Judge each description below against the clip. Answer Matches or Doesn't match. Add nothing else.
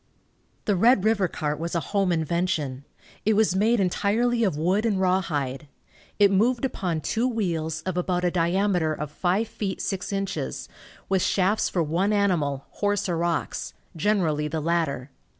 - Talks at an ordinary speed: Matches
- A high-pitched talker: Doesn't match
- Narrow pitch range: Doesn't match